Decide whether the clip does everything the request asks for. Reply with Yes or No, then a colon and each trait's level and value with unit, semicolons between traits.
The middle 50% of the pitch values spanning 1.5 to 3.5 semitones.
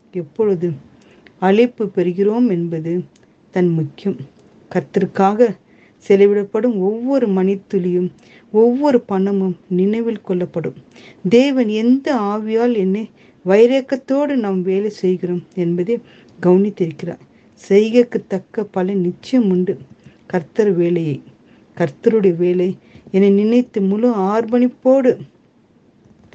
No: average, 4.0 semitones